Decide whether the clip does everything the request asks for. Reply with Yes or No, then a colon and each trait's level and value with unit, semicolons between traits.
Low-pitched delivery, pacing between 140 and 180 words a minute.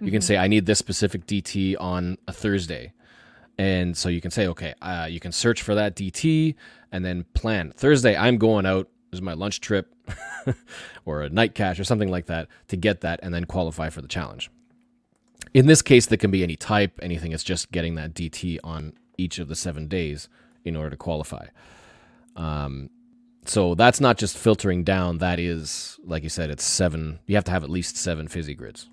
No: very low, 90 Hz; fast, 205 wpm